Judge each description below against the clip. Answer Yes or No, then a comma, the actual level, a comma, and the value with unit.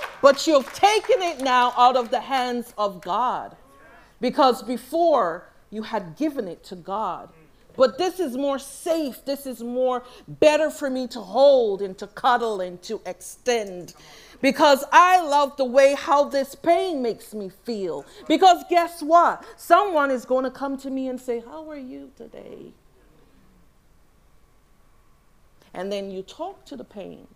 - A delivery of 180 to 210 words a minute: No, average, 160 wpm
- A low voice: No, very high, 265 Hz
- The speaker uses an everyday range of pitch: Yes, average, 4.5 semitones